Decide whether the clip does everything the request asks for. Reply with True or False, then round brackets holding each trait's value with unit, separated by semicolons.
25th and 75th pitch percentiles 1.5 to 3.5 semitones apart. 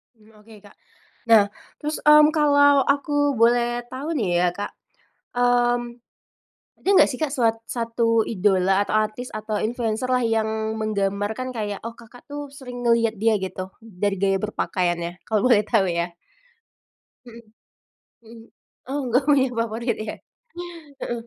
True (2.9 semitones)